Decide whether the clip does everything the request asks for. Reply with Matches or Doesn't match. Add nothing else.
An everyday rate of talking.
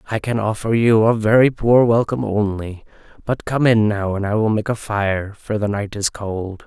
Doesn't match